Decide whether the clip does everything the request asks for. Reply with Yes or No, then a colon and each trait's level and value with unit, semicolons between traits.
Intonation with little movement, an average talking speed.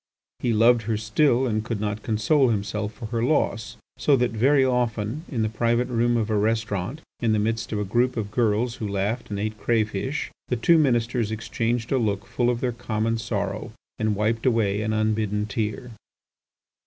Yes: narrow, 2.3 semitones; average, 190 wpm